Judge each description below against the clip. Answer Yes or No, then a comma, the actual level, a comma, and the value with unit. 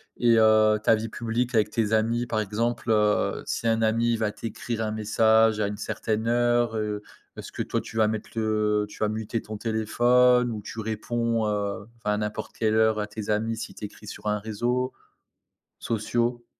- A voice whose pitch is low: Yes, low, 110 Hz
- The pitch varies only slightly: Yes, narrow, 1.5 semitones